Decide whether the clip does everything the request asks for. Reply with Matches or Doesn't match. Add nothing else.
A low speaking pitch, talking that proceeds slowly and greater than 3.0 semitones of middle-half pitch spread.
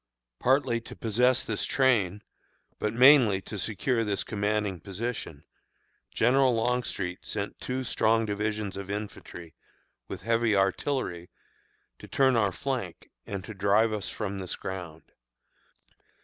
Matches